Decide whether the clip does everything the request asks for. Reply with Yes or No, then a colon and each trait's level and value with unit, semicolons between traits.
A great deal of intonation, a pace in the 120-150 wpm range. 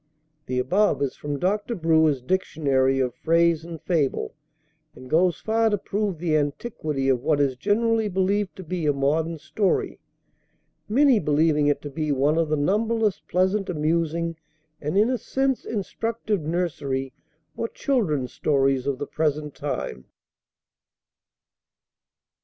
Yes: wide, 5.9 semitones; average, 140 wpm